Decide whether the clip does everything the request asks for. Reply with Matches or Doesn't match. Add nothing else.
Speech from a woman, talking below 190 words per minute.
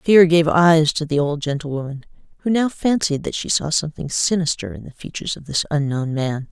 Doesn't match